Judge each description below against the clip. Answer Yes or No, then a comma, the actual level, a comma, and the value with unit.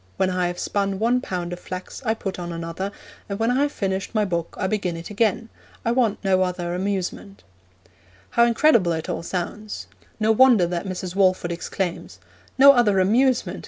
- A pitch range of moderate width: Yes, average, 3.8 semitones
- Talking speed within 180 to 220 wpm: Yes, average, 185 wpm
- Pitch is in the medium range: No, high, 195 Hz